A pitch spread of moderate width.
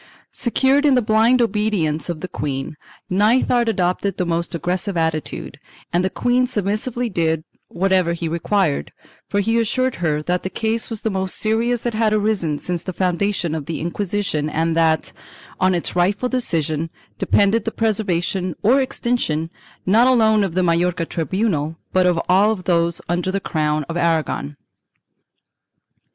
Yes: average, 4.7 semitones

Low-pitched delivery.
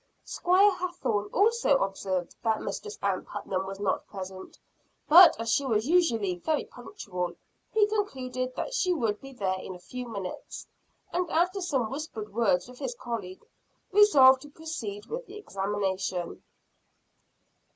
No: high, 245 Hz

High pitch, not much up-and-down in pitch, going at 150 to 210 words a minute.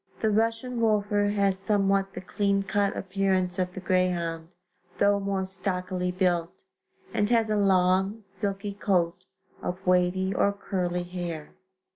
No: high, 195 Hz; narrow, 1.9 semitones; slow, 135 wpm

